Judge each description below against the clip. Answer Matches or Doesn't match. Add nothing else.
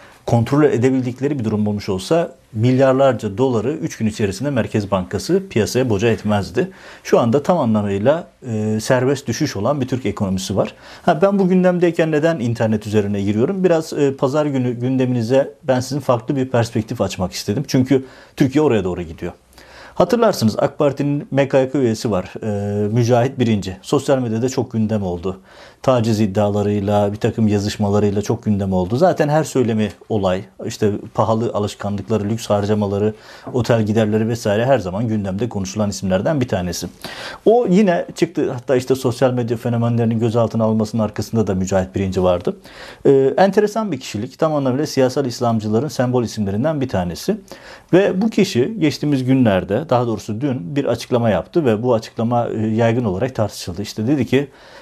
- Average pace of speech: Doesn't match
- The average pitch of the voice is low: Matches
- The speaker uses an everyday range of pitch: Matches